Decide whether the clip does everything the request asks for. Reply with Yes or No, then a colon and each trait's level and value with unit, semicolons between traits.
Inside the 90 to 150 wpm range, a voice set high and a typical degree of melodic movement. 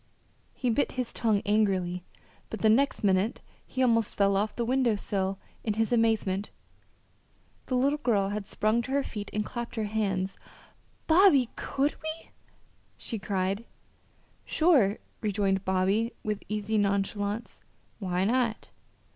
Yes: average, 140 wpm; high, 215 Hz; average, 3.2 semitones